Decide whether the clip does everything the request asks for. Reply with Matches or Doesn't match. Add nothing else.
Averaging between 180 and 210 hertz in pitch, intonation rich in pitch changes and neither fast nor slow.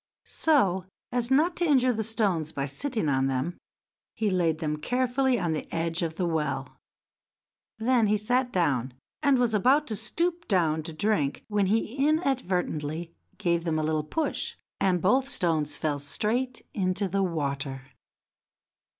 Matches